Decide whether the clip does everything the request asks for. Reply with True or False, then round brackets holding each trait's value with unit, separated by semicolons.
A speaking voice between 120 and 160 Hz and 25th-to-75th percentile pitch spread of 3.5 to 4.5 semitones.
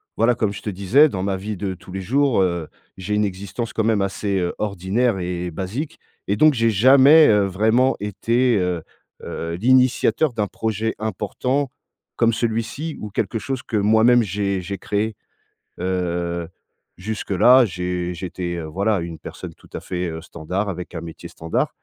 False (100 Hz; 4.1 semitones)